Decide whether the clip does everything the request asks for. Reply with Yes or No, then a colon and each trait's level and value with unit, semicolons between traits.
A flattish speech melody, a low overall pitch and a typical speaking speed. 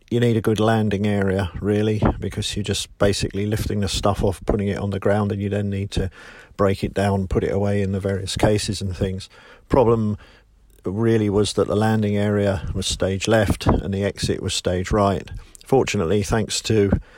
Yes: narrow, 1.4 semitones; low, 100 Hz; average, 195 wpm